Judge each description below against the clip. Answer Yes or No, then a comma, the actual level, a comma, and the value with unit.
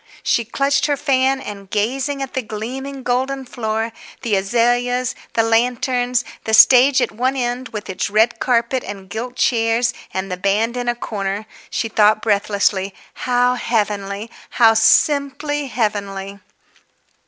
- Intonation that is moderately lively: Yes, average, 3.3 semitones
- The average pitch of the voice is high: Yes, high, 235 Hz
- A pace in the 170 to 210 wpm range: No, average, 140 wpm